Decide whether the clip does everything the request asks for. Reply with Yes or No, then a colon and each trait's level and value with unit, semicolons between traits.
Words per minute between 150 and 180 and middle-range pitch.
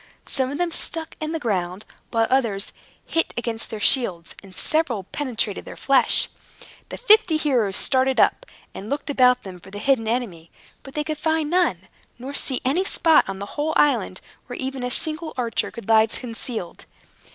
No: average, 175 wpm; very high, 255 Hz